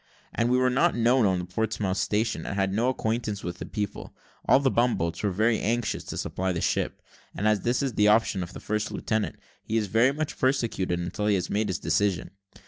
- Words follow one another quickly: Yes, fast, 230 wpm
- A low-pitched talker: Yes, low, 105 Hz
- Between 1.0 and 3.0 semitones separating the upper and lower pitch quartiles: No, average, 3.7 semitones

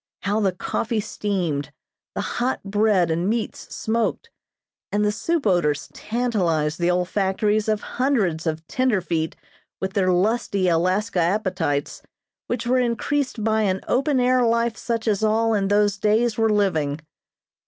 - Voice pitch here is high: Yes, high, 210 Hz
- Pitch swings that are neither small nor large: Yes, average, 4.1 semitones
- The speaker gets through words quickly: No, average, 145 wpm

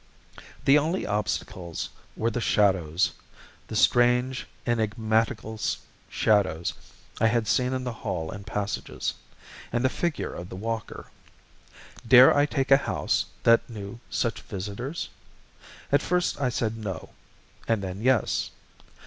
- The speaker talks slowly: Yes, slow, 130 wpm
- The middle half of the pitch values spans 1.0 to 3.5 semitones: No, average, 4.0 semitones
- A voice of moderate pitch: No, low, 115 Hz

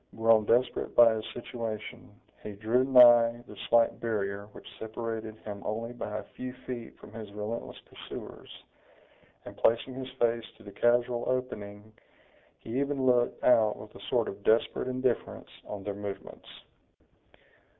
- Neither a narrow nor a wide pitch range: No, narrow, 2.3 semitones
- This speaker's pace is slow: No, average, 150 wpm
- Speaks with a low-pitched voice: Yes, low, 115 Hz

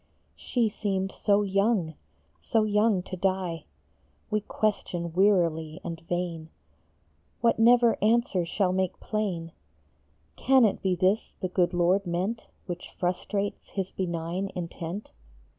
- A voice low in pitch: No, high, 190 Hz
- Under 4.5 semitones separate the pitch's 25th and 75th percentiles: Yes, average, 3.2 semitones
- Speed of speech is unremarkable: No, slow, 125 wpm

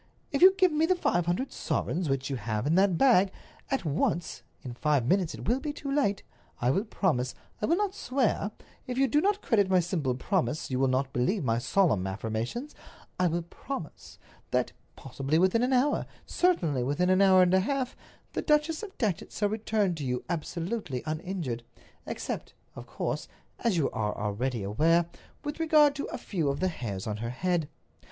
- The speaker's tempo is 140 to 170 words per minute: No, average, 180 wpm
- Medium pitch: Yes, medium, 180 Hz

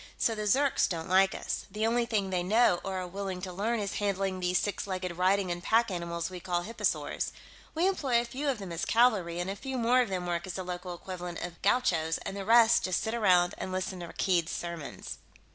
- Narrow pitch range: No, average, 4.0 semitones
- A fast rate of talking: Yes, fast, 230 wpm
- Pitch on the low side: No, high, 190 Hz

